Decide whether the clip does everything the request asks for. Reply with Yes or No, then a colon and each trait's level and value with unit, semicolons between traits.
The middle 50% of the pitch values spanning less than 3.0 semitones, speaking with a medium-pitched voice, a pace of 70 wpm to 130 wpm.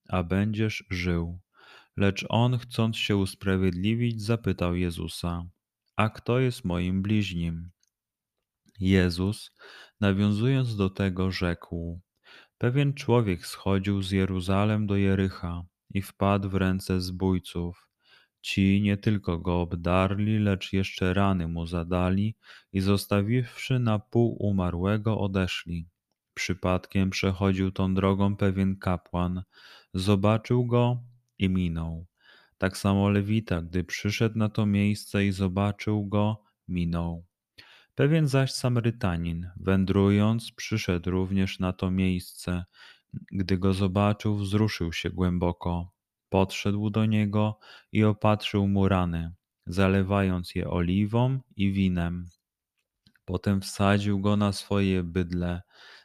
No: narrow, 2.6 semitones; very low, 95 Hz; slow, 110 wpm